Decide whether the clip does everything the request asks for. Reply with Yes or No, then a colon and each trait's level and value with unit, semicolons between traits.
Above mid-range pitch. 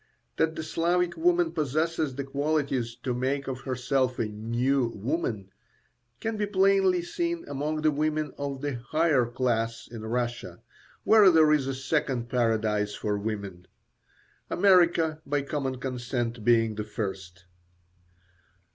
No: low, 135 Hz